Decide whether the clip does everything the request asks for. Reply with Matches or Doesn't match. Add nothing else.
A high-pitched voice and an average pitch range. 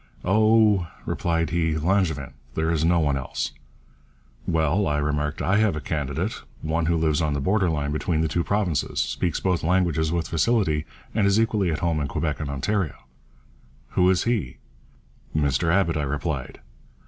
Doesn't match